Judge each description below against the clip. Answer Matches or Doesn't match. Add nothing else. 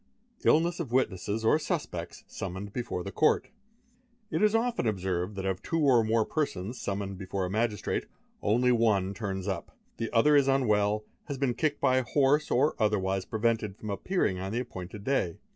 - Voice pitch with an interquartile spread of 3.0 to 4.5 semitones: Doesn't match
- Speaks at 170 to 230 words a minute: Matches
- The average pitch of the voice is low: Matches